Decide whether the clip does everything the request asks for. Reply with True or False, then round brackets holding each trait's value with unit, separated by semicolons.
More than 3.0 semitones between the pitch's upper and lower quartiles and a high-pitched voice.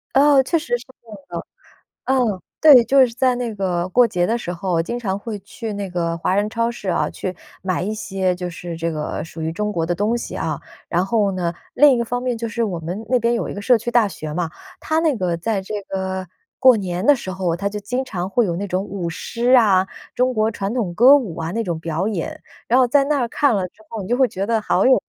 True (4.8 semitones; 205 Hz)